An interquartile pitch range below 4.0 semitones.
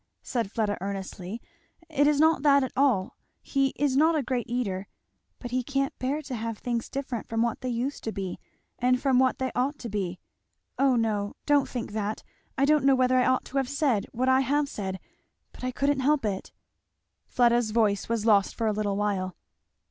No: average, 4.3 semitones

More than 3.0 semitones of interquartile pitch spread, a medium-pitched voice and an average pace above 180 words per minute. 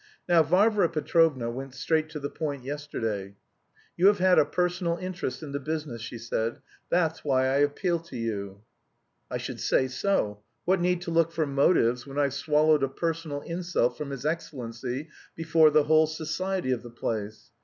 No: average, 4.5 semitones; medium, 150 Hz; average, 175 wpm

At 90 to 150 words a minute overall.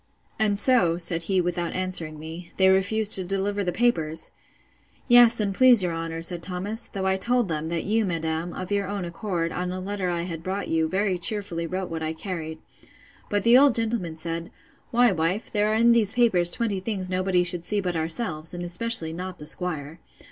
No: average, 200 wpm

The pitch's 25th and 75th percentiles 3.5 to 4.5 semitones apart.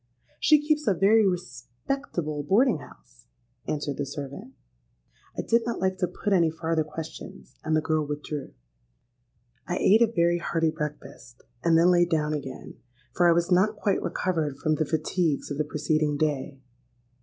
Yes: average, 3.8 semitones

